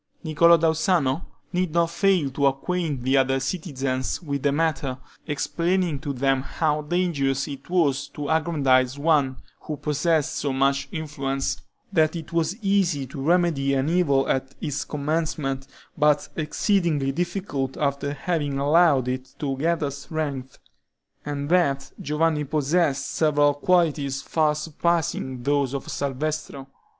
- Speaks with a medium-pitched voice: Yes, medium, 145 Hz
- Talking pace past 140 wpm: No, slow, 135 wpm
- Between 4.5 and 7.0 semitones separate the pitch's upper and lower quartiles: No, average, 3.2 semitones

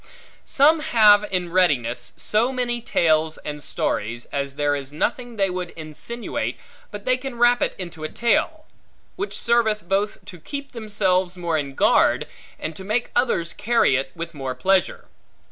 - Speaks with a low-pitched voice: No, high, 190 Hz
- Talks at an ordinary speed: Yes, average, 160 wpm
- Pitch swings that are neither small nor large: No, wide, 7.2 semitones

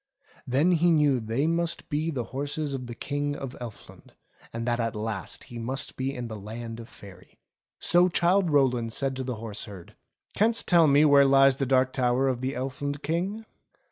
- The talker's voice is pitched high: No, low, 135 Hz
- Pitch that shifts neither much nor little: Yes, average, 3.8 semitones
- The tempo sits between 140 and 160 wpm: No, average, 195 wpm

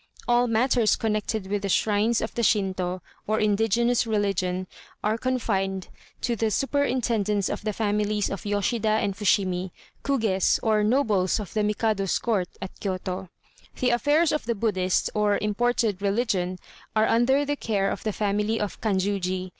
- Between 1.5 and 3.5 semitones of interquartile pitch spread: Yes, average, 2.9 semitones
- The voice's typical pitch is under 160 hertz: No, high, 210 Hz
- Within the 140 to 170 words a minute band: Yes, average, 155 wpm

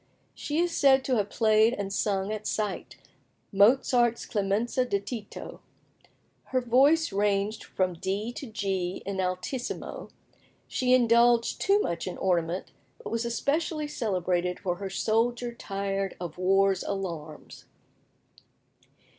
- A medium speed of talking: No, slow, 125 wpm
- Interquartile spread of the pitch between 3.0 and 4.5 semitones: Yes, average, 4.1 semitones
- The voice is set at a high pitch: Yes, high, 210 Hz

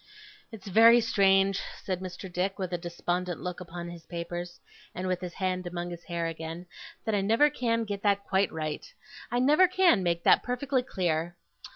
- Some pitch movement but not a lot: Yes, average, 4.0 semitones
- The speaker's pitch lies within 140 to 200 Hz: Yes, medium, 185 Hz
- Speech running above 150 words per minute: Yes, average, 185 wpm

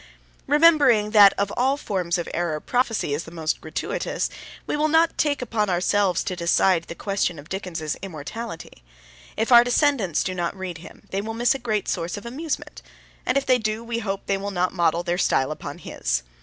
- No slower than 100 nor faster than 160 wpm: No, average, 195 wpm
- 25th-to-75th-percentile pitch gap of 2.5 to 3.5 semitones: No, wide, 5.6 semitones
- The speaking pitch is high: Yes, high, 200 Hz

